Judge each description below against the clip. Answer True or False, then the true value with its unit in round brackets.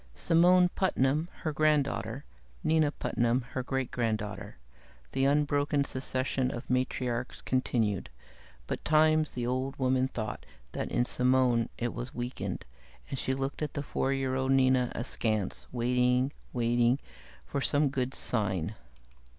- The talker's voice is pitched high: False (130 Hz)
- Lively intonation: False (2.6 semitones)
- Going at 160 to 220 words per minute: False (135 wpm)